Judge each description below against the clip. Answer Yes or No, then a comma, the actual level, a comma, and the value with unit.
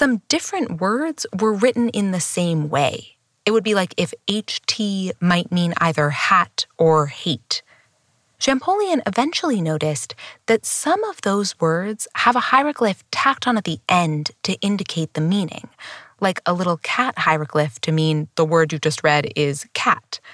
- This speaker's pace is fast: No, average, 160 wpm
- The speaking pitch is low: No, medium, 185 Hz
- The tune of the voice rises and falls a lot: Yes, wide, 6.9 semitones